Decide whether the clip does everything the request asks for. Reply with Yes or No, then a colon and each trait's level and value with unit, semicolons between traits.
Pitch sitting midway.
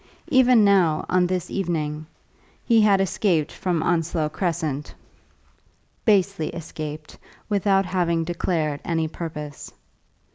Yes: medium, 170 Hz